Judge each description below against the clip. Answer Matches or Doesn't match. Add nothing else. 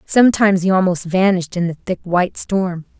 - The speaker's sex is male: Doesn't match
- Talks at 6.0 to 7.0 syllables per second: Doesn't match